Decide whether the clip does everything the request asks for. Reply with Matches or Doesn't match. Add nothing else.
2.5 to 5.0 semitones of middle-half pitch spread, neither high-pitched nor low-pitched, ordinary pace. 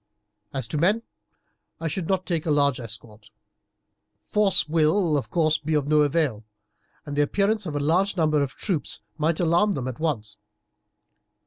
Matches